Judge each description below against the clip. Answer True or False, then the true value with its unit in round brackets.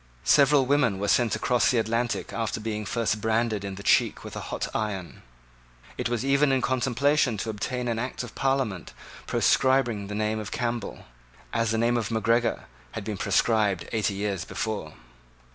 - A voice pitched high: False (115 Hz)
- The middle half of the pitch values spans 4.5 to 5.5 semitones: False (2.8 semitones)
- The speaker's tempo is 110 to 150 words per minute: False (175 wpm)